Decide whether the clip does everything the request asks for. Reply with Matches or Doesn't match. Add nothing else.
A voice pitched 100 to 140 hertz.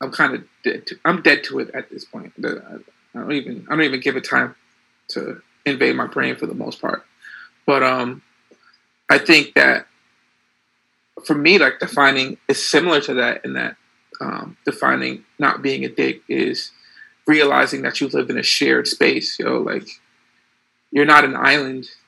Matches